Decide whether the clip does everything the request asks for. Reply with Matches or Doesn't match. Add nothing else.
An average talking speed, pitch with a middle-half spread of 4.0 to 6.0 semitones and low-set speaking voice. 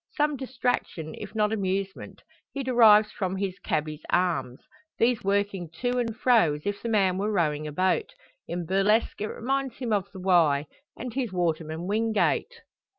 Doesn't match